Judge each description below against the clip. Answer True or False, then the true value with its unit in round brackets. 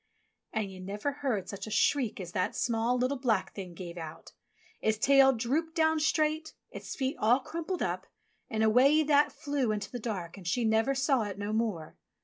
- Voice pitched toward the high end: True (235 Hz)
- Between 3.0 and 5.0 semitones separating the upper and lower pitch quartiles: False (5.6 semitones)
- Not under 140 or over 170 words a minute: False (190 wpm)